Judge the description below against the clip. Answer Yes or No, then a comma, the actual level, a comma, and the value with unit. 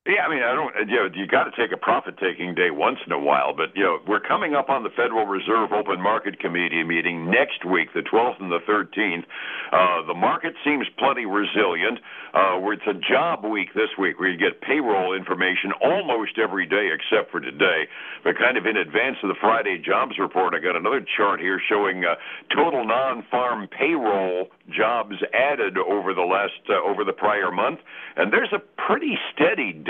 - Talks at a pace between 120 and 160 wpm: No, average, 200 wpm